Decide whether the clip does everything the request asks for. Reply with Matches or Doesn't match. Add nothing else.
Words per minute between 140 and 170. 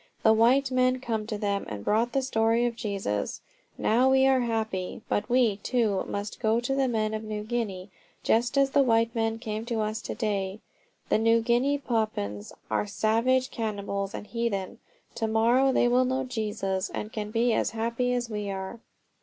Doesn't match